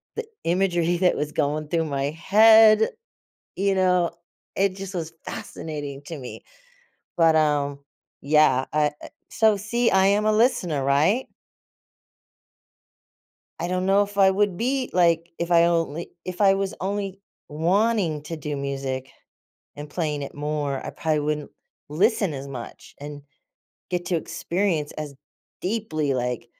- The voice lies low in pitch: No, medium, 170 Hz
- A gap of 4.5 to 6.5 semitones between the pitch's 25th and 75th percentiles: Yes, average, 4.8 semitones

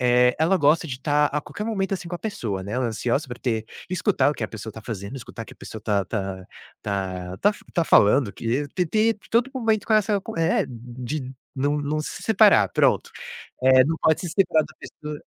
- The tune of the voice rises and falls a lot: Yes, wide, 6.9 semitones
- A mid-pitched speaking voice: Yes, medium, 145 Hz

